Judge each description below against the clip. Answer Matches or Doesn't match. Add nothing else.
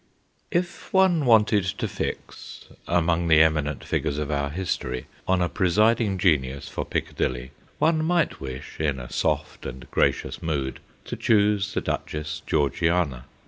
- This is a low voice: Matches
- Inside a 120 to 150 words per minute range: Matches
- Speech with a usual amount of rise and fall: Doesn't match